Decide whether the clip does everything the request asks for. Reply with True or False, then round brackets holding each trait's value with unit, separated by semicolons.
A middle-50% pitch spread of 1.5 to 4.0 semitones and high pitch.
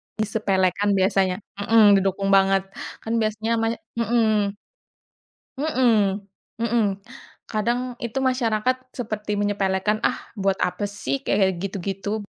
True (2.8 semitones; 210 Hz)